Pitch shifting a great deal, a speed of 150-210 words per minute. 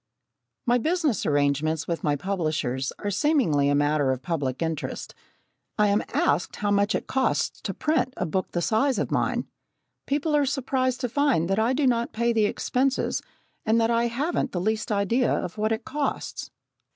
Yes: wide, 7.9 semitones; average, 180 wpm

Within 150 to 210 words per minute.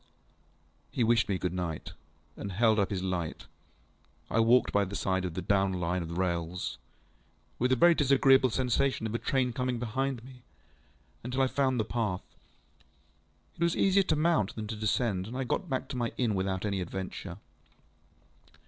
Yes: average, 180 wpm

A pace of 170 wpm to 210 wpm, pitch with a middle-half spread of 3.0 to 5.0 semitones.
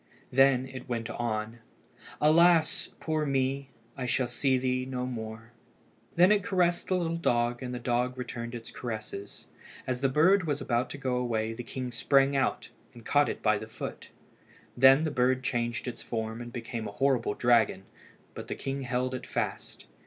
No: average, 180 wpm; narrow, 2.5 semitones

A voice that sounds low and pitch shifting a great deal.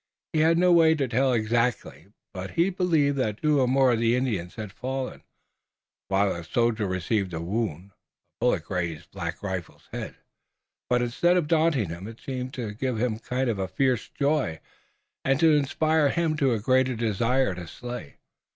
Yes: low, 120 Hz; wide, 5.7 semitones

